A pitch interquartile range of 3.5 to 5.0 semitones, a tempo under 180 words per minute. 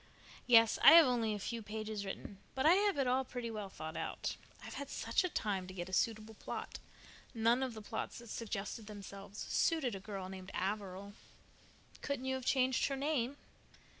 No: average, 4.5 semitones; average, 195 wpm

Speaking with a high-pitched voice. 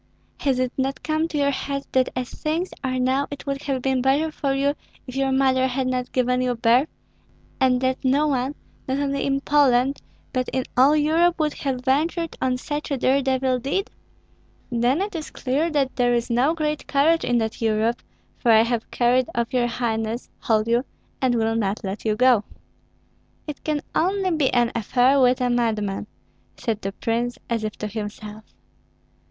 Yes: very high, 260 Hz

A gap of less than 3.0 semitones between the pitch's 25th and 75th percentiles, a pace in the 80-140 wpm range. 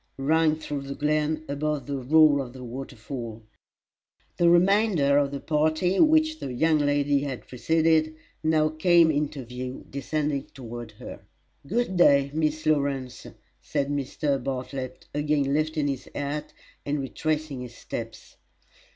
Yes: narrow, 2.5 semitones; slow, 135 wpm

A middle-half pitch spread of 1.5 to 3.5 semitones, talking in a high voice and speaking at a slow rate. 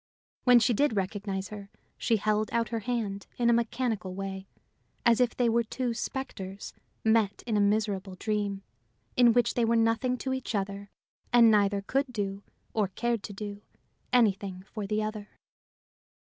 No: average, 2.9 semitones; high, 215 Hz; average, 165 wpm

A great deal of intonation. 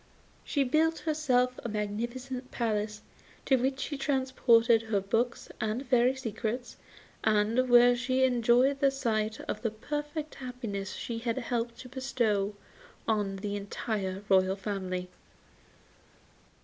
No: average, 3.6 semitones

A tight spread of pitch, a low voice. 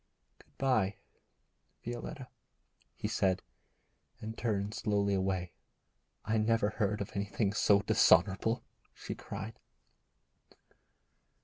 Yes: narrow, 2.2 semitones; low, 105 Hz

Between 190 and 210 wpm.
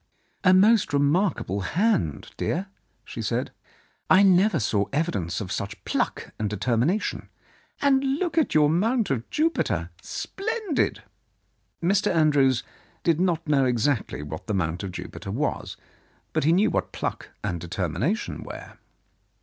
No: average, 140 wpm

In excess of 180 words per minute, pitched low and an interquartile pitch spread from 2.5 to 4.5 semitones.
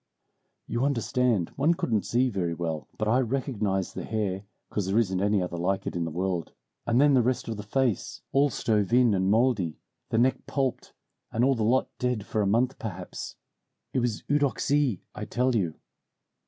No: average, 190 wpm; low, 110 Hz; average, 4.9 semitones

